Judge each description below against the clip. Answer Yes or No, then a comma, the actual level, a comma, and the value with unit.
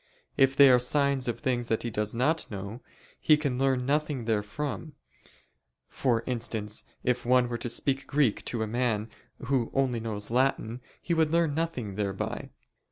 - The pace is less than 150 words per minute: No, average, 165 wpm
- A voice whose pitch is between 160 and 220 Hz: No, low, 125 Hz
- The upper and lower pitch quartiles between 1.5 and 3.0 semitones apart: No, average, 3.5 semitones